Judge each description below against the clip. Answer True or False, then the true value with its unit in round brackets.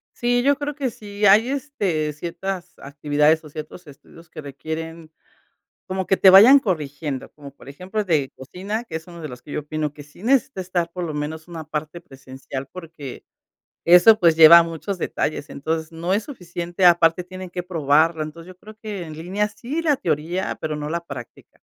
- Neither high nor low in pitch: True (170 Hz)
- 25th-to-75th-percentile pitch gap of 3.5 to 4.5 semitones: True (4.0 semitones)